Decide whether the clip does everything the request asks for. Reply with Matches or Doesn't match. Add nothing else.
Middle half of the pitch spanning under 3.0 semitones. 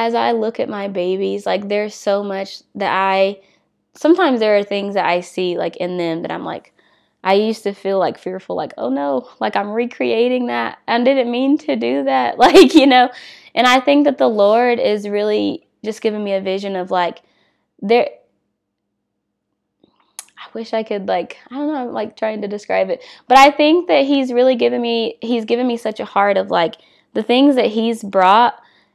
Doesn't match